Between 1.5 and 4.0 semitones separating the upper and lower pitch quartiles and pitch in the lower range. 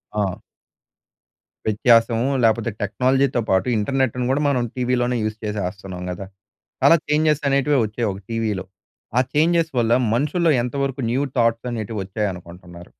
No: average, 4.5 semitones; low, 115 Hz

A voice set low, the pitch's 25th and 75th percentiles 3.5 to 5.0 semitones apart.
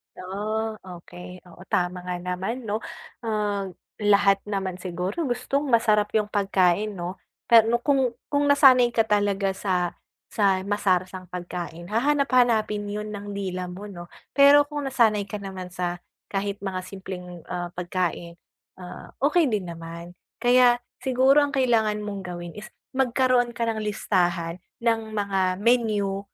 No: high, 205 Hz; average, 4.2 semitones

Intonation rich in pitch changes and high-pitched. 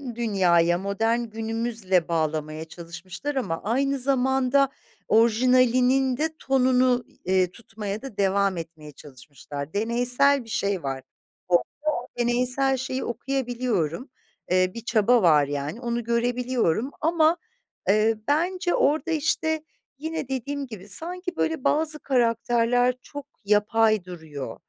Yes: wide, 6.1 semitones; high, 235 Hz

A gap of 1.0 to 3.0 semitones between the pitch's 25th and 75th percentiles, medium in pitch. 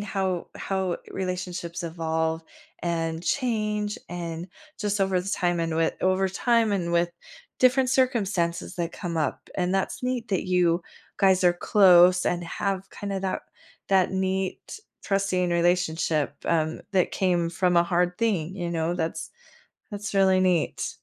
Yes: narrow, 2.4 semitones; medium, 180 Hz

